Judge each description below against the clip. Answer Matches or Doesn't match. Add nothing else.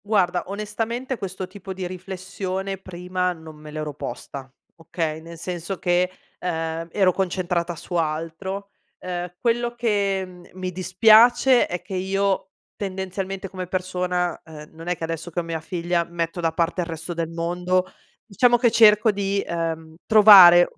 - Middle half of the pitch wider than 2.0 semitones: Matches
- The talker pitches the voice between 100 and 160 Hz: Doesn't match